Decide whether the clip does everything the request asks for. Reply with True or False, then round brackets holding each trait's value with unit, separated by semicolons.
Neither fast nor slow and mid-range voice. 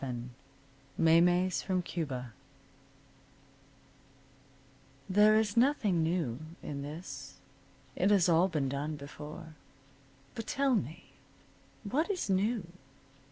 False (100 wpm; 175 Hz)